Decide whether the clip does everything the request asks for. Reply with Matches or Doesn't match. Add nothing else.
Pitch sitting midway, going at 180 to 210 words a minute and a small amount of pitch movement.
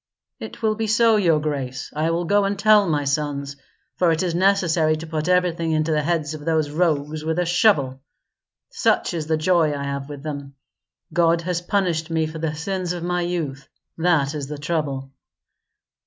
Doesn't match